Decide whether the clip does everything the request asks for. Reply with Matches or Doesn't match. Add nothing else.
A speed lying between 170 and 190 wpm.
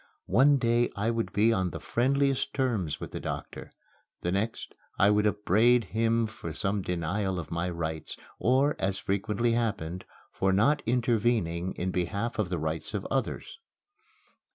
Doesn't match